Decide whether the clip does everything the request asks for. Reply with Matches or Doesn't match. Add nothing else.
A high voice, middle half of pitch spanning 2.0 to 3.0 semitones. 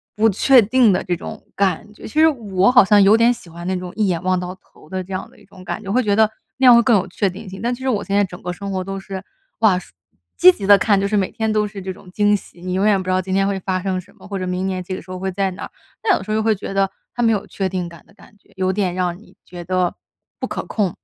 Matches